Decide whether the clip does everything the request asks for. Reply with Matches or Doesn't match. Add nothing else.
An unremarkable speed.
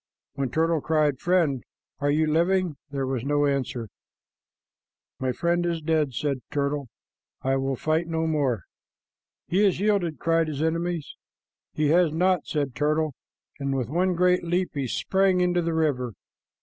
Matches